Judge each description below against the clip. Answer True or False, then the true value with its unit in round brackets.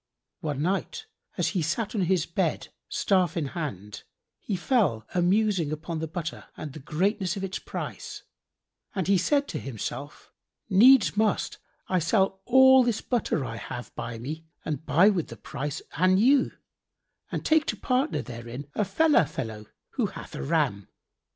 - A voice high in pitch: False (175 Hz)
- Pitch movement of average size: False (6.4 semitones)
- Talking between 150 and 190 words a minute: True (165 wpm)